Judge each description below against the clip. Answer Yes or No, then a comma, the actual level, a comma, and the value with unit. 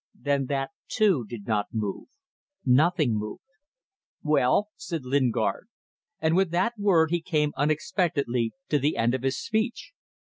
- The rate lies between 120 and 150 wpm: Yes, average, 140 wpm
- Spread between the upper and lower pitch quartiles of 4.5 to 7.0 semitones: Yes, average, 5.3 semitones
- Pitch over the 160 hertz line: No, medium, 145 Hz